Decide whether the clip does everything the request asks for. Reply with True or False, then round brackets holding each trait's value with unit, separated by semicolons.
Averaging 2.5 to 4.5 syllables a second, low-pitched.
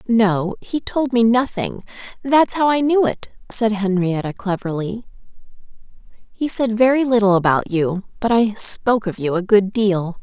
False (4.4 syllables/s; 215 Hz)